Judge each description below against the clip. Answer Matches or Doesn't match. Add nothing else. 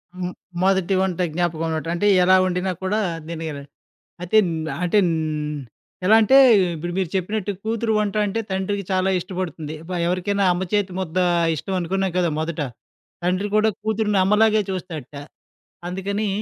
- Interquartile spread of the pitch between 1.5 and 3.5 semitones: Matches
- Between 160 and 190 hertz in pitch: Matches